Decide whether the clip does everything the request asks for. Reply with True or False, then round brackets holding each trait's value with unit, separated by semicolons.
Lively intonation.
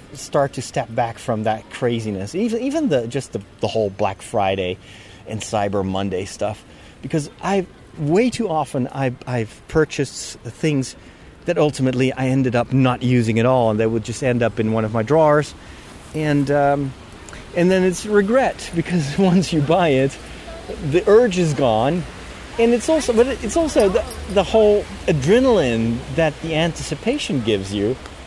True (7.4 semitones)